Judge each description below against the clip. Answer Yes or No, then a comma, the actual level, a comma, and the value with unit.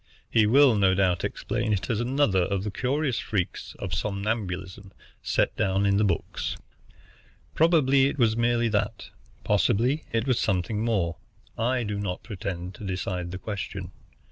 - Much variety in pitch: No, average, 3.9 semitones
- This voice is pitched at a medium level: No, low, 105 Hz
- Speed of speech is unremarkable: Yes, average, 155 wpm